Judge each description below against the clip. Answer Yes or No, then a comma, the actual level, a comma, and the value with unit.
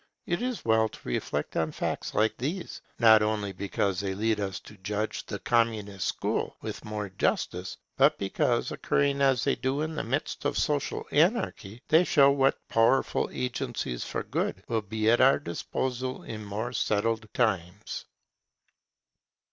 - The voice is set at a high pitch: No, low, 110 Hz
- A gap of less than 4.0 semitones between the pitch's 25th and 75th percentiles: No, average, 4.7 semitones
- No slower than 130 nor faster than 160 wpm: Yes, average, 155 wpm